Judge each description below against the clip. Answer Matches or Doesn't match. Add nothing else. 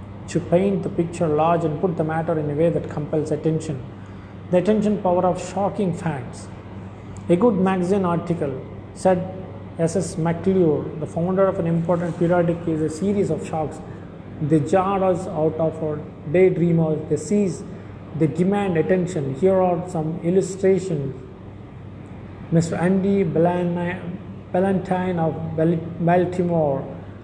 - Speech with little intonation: Doesn't match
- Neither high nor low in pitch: Matches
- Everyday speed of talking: Doesn't match